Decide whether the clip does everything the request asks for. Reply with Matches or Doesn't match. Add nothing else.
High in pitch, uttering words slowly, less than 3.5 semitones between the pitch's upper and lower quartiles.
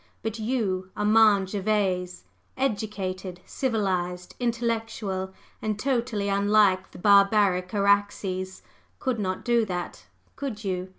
Matches